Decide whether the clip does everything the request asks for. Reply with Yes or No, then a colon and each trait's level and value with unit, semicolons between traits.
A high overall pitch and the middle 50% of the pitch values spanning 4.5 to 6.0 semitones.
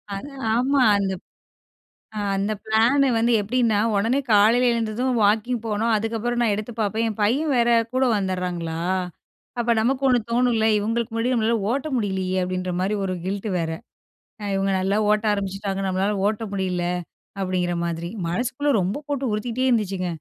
No: high, 215 Hz; average, 3.7 semitones